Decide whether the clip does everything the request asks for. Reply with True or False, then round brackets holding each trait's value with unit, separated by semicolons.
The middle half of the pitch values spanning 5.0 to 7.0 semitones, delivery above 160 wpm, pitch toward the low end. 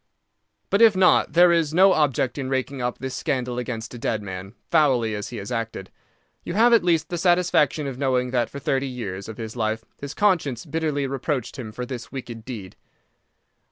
True (5.3 semitones; 195 wpm; 130 Hz)